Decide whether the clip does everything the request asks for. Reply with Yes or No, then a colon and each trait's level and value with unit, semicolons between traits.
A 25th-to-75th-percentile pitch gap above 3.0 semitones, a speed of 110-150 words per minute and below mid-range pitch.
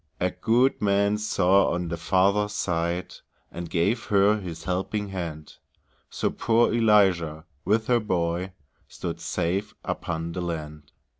Yes: average, 3.6 semitones; slow, 135 wpm; very low, 95 Hz